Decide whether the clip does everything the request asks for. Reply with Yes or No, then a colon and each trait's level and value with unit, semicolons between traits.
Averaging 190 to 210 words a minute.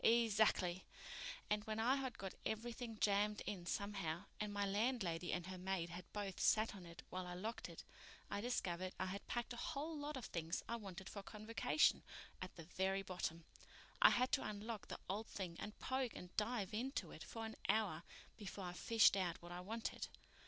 Yes: average, 195 wpm